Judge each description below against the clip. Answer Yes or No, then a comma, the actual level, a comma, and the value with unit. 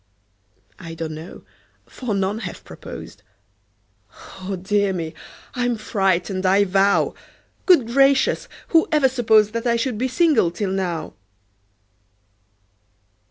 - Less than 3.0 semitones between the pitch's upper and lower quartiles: No, average, 4.7 semitones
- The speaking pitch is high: Yes, high, 205 Hz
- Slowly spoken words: Yes, slow, 115 wpm